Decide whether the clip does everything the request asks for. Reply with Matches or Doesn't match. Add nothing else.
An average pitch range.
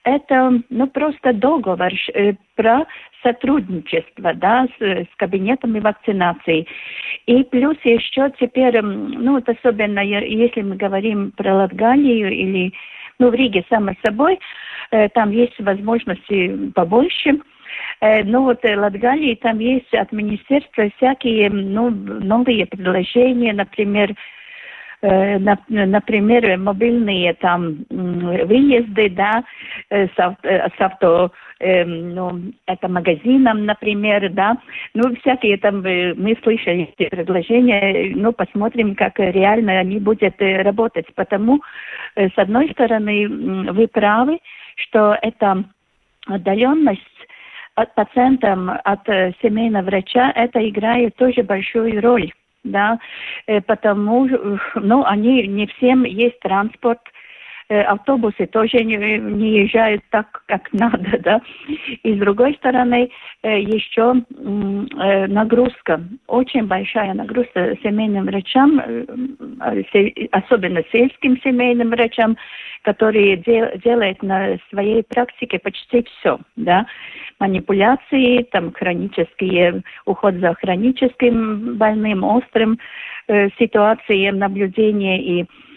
Matches